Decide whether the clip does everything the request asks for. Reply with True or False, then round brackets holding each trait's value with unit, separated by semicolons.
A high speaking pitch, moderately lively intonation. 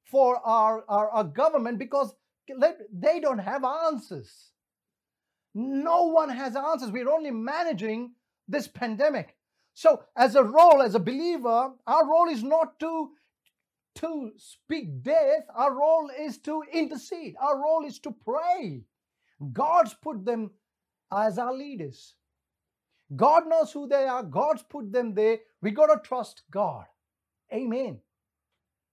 False (270 Hz; 5.7 semitones)